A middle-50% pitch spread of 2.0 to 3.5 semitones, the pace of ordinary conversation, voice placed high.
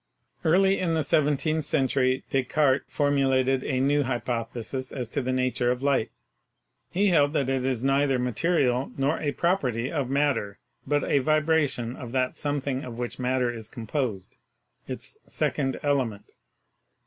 No: narrow, 2.6 semitones; average, 150 wpm; low, 135 Hz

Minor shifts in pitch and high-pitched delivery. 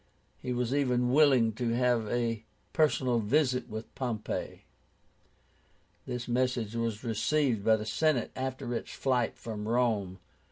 No: narrow, 2.3 semitones; low, 120 Hz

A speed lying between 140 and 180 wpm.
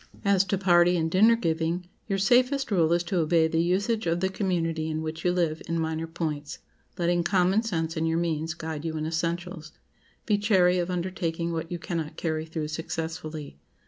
No: average, 190 wpm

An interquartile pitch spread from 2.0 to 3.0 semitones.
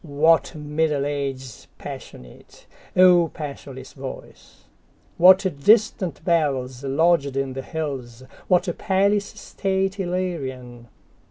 No: average, 5.3 semitones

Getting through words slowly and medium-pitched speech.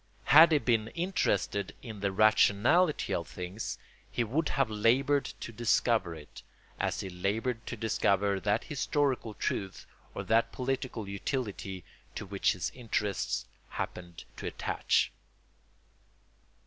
No: slow, 125 wpm; low, 110 Hz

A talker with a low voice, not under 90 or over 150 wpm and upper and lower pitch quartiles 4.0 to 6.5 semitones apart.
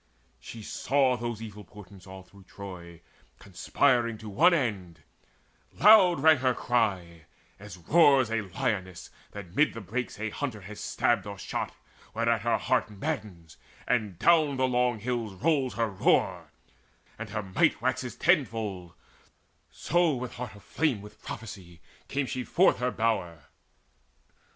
Yes: low, 110 Hz; average, 140 wpm; average, 4.7 semitones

